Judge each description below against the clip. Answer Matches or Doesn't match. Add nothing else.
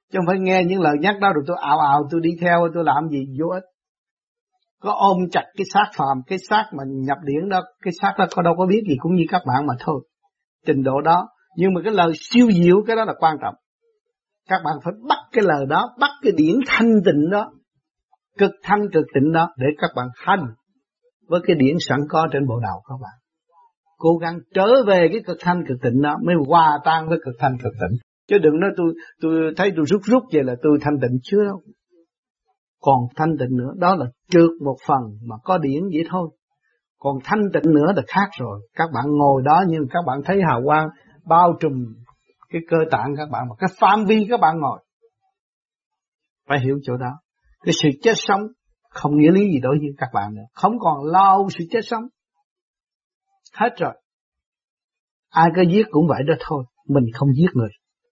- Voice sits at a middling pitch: Matches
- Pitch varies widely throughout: Matches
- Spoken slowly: Doesn't match